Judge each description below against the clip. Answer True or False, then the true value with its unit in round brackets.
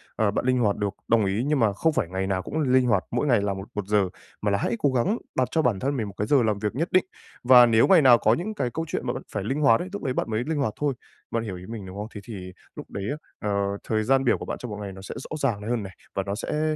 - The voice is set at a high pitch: False (115 Hz)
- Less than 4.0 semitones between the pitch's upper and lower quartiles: False (5.0 semitones)